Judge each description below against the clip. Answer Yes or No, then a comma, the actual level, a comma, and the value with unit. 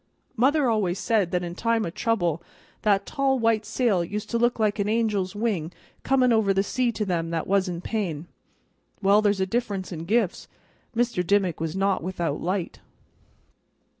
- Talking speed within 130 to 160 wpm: No, average, 175 wpm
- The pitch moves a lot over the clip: No, average, 4.2 semitones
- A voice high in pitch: Yes, high, 200 Hz